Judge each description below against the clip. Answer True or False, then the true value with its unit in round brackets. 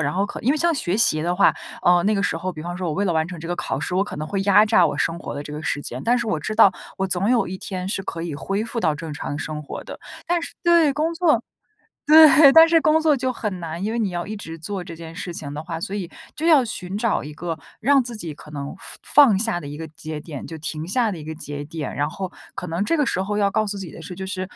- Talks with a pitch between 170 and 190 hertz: True (185 Hz)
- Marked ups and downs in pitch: True (5.8 semitones)